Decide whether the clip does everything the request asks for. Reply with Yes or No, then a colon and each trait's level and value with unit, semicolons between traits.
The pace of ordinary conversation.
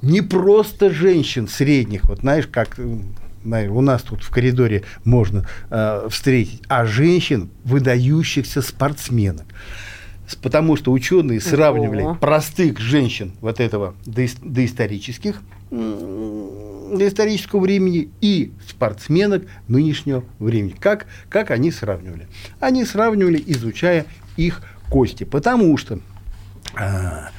No: slow, 105 wpm